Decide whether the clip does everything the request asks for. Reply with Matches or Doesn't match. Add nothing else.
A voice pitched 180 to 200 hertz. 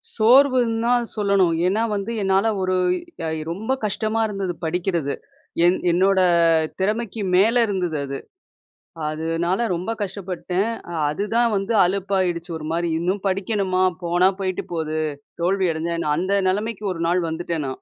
Matches